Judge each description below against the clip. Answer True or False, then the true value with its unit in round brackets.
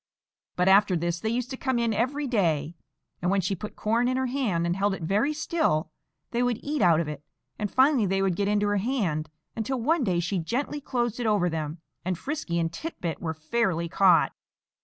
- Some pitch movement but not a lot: False (6.2 semitones)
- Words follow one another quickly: True (220 wpm)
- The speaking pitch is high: True (205 Hz)